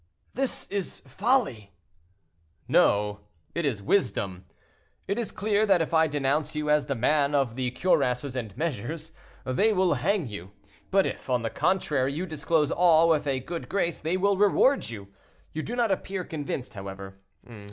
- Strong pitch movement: Yes, wide, 7.0 semitones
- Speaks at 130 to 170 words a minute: Yes, average, 165 wpm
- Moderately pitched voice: Yes, medium, 150 Hz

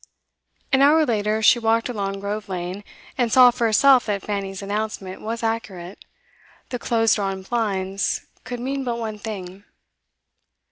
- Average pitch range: Yes, average, 3.1 semitones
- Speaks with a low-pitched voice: No, high, 215 Hz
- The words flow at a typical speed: Yes, average, 145 wpm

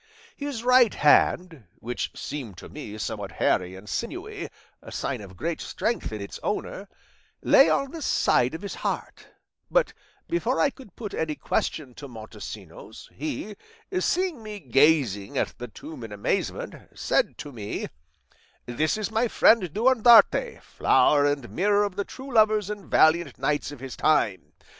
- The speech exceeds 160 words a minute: No, average, 155 wpm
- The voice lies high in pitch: No, medium, 160 Hz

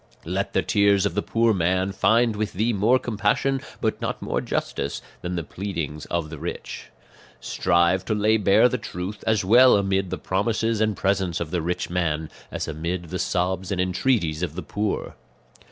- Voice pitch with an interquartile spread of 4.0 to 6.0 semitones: No, average, 3.5 semitones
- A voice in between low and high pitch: No, very low, 95 Hz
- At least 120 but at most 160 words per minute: No, average, 185 wpm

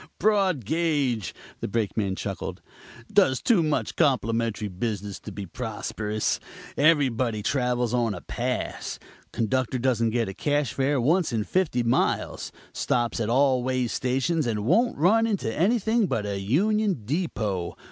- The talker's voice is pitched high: No, low, 125 Hz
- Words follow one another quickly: No, average, 140 wpm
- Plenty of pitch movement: Yes, wide, 5.9 semitones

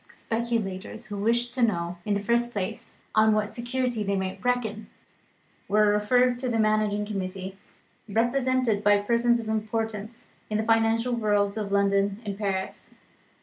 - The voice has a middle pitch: No, high, 215 Hz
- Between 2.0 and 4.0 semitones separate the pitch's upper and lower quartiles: Yes, average, 2.7 semitones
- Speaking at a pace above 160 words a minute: No, average, 150 wpm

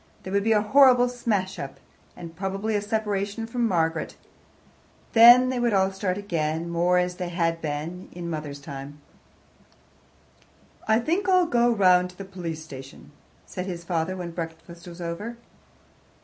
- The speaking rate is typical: Yes, average, 165 wpm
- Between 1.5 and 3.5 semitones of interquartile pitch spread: No, average, 4.6 semitones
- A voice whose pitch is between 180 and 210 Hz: Yes, medium, 185 Hz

